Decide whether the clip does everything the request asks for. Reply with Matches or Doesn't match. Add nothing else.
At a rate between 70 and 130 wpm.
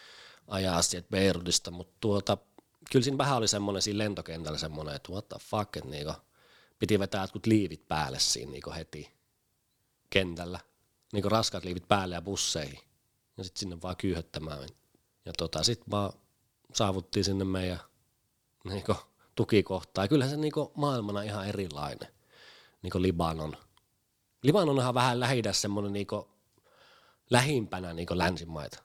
Doesn't match